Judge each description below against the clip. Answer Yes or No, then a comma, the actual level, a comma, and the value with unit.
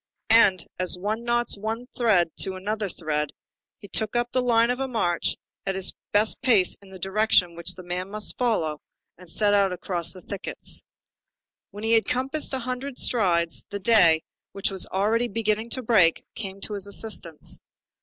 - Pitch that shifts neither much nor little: Yes, average, 3.9 semitones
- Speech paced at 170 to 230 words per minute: Yes, average, 175 wpm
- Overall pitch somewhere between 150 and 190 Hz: No, high, 205 Hz